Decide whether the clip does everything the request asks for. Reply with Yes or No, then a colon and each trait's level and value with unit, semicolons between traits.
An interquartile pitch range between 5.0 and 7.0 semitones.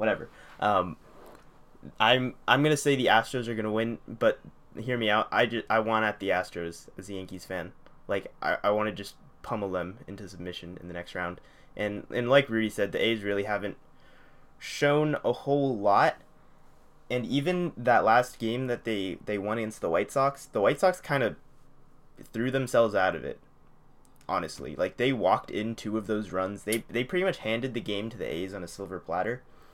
No: average, 4.0 semitones